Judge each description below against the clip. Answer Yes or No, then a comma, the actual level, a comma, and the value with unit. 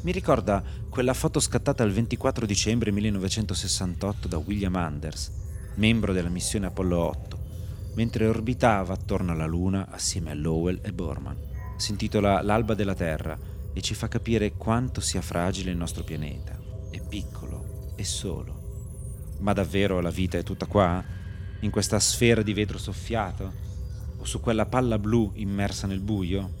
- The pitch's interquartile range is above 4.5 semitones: No, average, 2.9 semitones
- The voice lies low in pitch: Yes, low, 100 Hz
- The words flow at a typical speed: Yes, average, 150 wpm